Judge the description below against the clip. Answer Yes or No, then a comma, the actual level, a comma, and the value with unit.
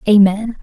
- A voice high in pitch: Yes, high, 210 Hz